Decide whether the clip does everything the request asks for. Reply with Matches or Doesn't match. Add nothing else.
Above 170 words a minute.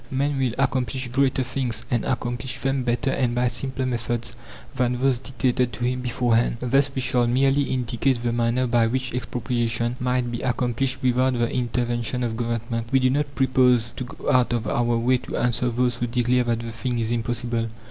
Matches